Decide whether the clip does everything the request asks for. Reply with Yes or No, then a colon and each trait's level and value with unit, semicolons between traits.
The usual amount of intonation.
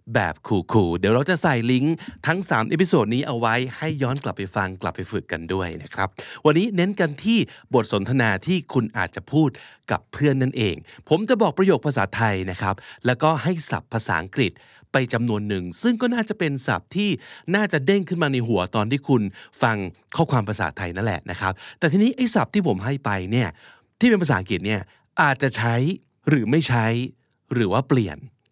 No: wide, 7.6 semitones